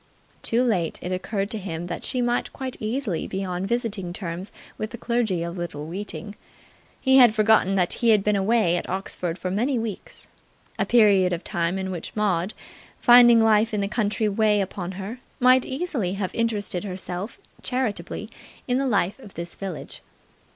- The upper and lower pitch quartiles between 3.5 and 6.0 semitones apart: Yes, average, 4.0 semitones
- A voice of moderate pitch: No, high, 205 Hz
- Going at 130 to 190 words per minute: Yes, average, 180 wpm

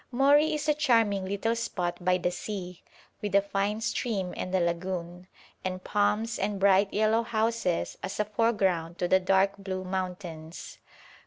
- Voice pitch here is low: No, high, 195 Hz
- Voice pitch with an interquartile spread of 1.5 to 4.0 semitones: Yes, average, 3.3 semitones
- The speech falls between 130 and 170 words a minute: Yes, average, 160 wpm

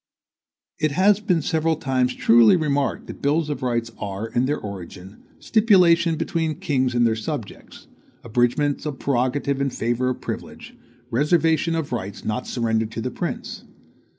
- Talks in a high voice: No, low, 135 Hz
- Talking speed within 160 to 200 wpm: No, average, 150 wpm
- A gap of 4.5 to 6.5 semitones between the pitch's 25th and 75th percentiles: Yes, average, 5.2 semitones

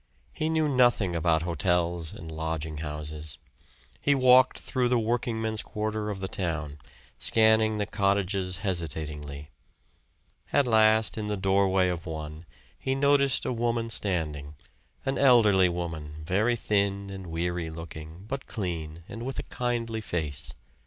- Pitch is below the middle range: Yes, very low, 95 Hz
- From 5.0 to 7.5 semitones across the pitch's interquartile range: Yes, wide, 5.6 semitones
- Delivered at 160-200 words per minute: No, average, 140 wpm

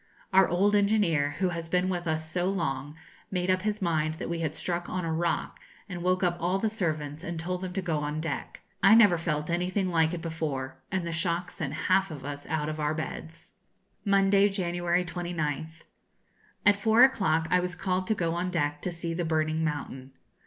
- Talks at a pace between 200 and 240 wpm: Yes, fast, 205 wpm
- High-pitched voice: No, medium, 170 Hz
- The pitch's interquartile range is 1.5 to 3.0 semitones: Yes, average, 2.7 semitones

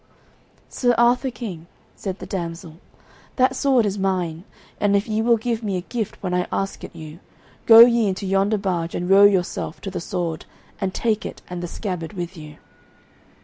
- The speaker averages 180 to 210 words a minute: Yes, average, 190 wpm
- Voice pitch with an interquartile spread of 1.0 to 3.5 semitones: No, average, 4.0 semitones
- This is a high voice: Yes, high, 195 Hz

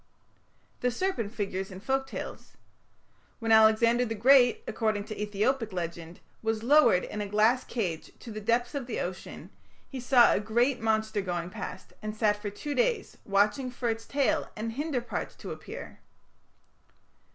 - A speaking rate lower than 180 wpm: Yes, average, 165 wpm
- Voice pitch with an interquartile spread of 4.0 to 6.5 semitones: No, average, 3.2 semitones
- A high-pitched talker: Yes, high, 225 Hz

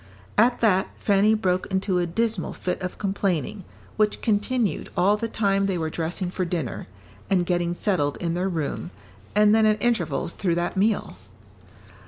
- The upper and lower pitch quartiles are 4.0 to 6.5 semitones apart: No, average, 3.2 semitones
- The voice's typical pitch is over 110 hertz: Yes, high, 190 Hz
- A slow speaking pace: No, average, 165 wpm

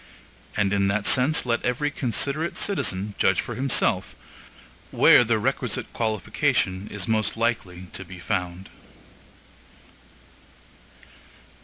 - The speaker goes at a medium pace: No, slow, 110 wpm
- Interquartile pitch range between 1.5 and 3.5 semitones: No, average, 4.5 semitones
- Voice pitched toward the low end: Yes, low, 110 Hz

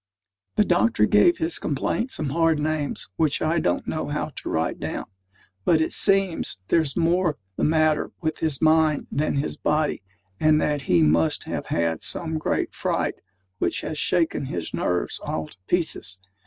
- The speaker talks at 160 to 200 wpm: Yes, average, 170 wpm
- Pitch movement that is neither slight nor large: No, wide, 5.9 semitones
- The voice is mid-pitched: Yes, medium, 155 Hz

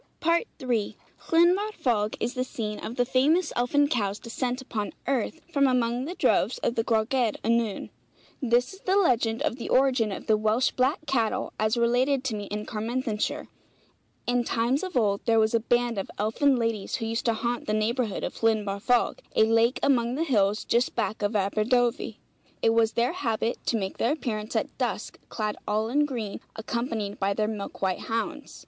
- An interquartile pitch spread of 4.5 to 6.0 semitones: No, average, 3.0 semitones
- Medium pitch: No, high, 235 Hz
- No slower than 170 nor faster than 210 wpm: Yes, average, 185 wpm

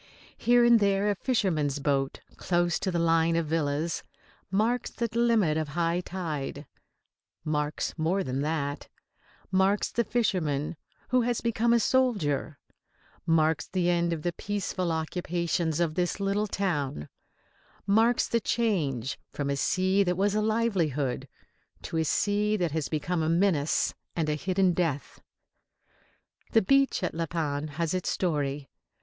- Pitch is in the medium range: Yes, medium, 175 Hz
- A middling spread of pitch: Yes, average, 4.8 semitones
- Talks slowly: No, average, 145 wpm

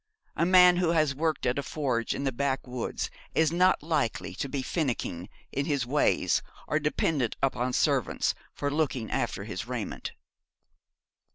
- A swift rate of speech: No, average, 155 wpm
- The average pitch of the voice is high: No, medium, 140 Hz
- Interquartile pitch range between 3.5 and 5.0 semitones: Yes, average, 4.0 semitones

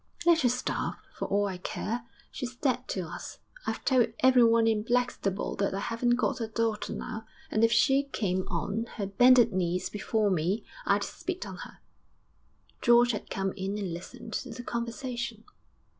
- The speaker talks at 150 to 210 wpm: Yes, average, 175 wpm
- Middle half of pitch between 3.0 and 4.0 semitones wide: Yes, average, 3.4 semitones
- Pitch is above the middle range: Yes, high, 225 Hz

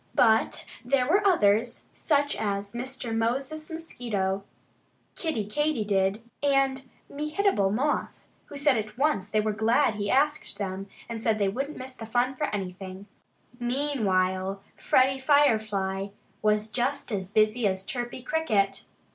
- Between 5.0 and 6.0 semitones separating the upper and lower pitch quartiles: Yes, wide, 5.4 semitones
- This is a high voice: Yes, high, 225 Hz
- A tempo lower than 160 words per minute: Yes, average, 140 wpm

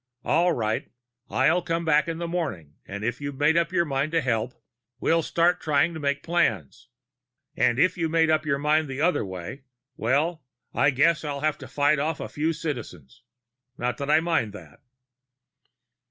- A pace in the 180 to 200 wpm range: Yes, average, 185 wpm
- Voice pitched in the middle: Yes, medium, 150 Hz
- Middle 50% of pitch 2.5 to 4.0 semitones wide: No, average, 4.4 semitones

